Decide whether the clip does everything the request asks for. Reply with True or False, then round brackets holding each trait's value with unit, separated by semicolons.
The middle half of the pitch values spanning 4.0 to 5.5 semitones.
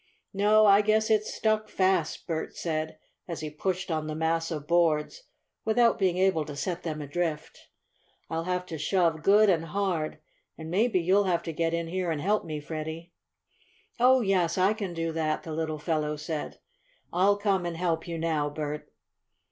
False (3.5 semitones)